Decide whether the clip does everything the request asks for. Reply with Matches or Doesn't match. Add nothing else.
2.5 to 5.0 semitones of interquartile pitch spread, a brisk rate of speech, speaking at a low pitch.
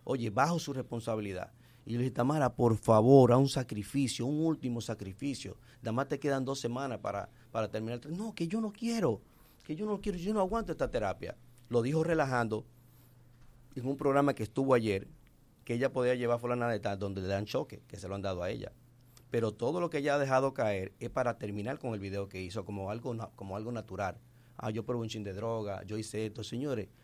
Matches